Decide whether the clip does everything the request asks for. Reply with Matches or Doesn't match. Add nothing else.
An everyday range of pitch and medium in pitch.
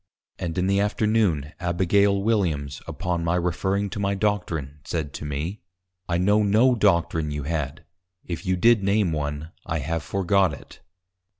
Doesn't match